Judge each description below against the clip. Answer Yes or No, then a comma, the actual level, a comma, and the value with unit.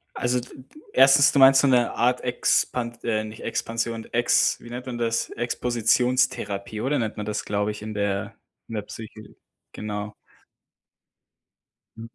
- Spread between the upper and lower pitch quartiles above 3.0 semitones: No, narrow, 2.5 semitones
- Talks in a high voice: No, low, 115 Hz